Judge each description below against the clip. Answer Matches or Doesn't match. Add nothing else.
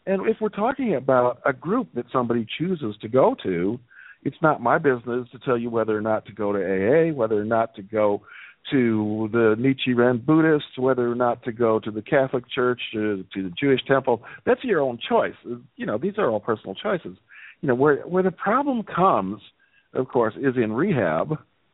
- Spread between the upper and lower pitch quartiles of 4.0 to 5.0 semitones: Matches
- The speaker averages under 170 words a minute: Doesn't match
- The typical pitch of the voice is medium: Doesn't match